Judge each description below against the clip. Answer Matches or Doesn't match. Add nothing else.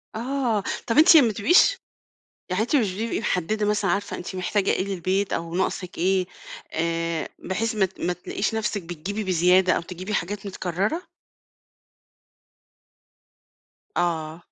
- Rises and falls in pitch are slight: Doesn't match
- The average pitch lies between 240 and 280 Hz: Doesn't match